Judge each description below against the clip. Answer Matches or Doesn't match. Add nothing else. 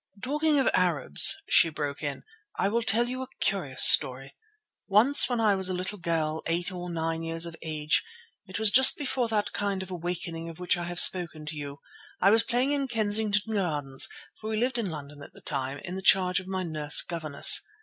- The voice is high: Doesn't match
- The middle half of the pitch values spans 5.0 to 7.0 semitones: Matches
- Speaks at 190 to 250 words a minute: Matches